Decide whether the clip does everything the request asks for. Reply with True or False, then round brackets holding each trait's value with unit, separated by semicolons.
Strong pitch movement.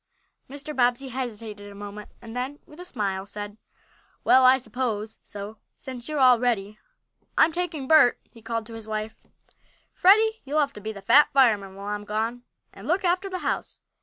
False (5.0 semitones)